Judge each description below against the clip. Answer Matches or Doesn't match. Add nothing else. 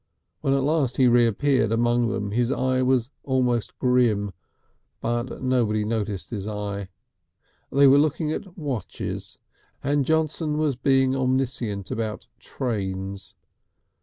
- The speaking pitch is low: Matches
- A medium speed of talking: Doesn't match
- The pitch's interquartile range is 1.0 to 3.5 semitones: Doesn't match